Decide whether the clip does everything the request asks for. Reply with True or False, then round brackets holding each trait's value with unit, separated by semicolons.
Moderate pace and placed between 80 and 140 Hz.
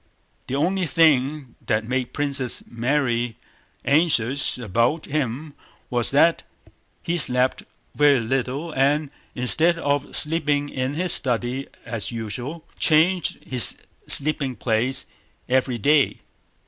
False (110 wpm; 135 Hz)